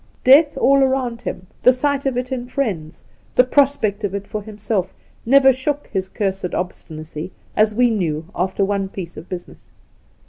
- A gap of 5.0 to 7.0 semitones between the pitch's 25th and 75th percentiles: Yes, wide, 5.6 semitones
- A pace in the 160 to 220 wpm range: Yes, average, 170 wpm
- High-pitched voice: Yes, high, 215 Hz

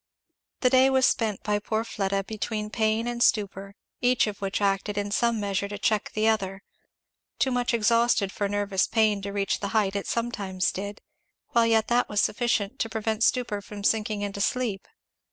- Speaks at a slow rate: No, average, 185 wpm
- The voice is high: Yes, high, 210 Hz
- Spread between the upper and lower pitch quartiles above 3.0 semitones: No, narrow, 2.4 semitones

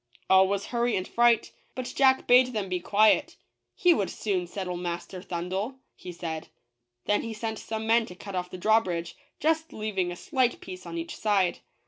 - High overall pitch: Yes, high, 200 Hz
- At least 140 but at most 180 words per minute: No, average, 190 wpm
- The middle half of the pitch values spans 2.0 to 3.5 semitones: No, average, 4.4 semitones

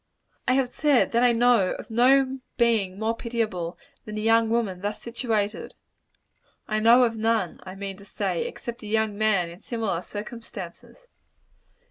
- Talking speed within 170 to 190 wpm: No, average, 160 wpm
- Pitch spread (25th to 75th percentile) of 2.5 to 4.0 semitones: Yes, average, 2.9 semitones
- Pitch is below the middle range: No, high, 220 Hz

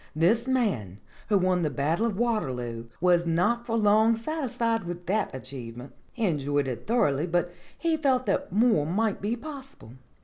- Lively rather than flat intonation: Yes, wide, 8.1 semitones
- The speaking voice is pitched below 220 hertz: Yes, high, 190 Hz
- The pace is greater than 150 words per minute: Yes, average, 170 wpm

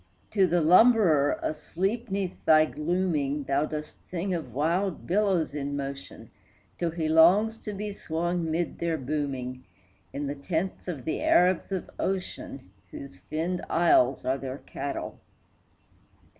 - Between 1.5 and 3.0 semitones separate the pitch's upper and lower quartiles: No, average, 4.5 semitones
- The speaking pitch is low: No, medium, 160 Hz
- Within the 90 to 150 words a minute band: Yes, average, 140 wpm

